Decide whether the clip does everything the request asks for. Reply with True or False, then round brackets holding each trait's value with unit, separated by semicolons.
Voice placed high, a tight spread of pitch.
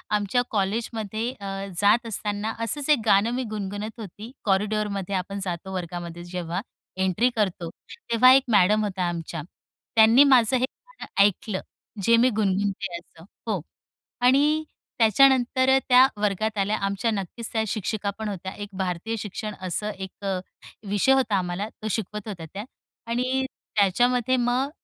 False (210 Hz; 3.6 semitones)